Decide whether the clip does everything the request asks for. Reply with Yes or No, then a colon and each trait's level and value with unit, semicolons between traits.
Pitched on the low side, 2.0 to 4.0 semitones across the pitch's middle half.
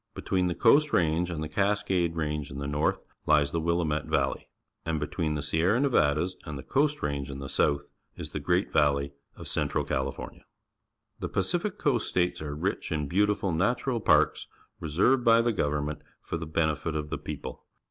No: very low, 80 Hz; average, 4.8 semitones